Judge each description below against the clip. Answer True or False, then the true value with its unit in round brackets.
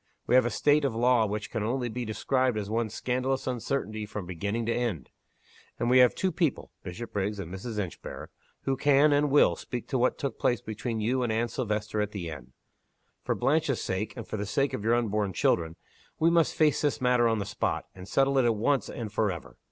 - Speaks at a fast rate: True (220 wpm)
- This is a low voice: True (115 Hz)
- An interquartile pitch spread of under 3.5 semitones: False (3.8 semitones)